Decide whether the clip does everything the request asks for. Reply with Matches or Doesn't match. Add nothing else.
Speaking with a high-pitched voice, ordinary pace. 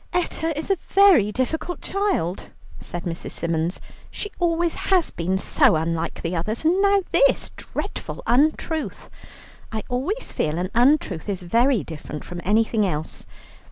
Matches